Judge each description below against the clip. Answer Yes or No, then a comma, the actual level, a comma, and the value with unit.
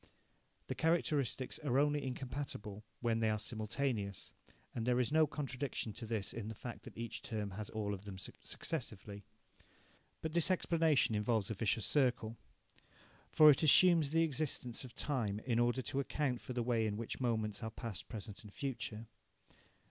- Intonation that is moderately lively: Yes, average, 4.5 semitones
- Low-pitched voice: Yes, low, 120 Hz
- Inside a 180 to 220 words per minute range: No, average, 170 wpm